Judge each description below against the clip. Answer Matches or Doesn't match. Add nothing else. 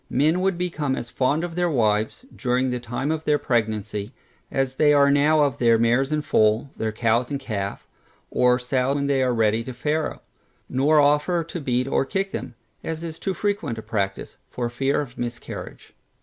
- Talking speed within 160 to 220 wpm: Matches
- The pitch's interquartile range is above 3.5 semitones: Matches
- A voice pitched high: Doesn't match